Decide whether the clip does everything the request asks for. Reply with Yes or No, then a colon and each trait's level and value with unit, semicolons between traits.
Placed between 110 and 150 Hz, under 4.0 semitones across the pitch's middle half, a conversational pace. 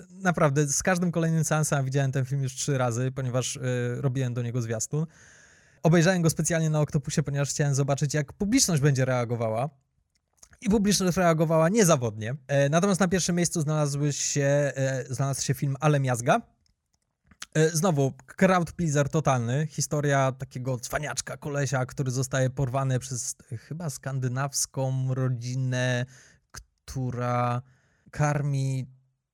Yes: medium, 140 Hz; average, 3.2 semitones; average, 135 wpm